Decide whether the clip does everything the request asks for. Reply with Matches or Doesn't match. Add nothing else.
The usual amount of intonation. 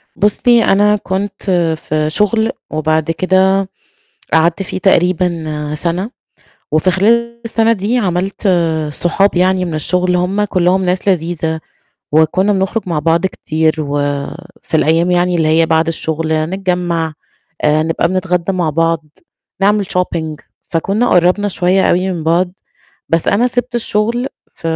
Matches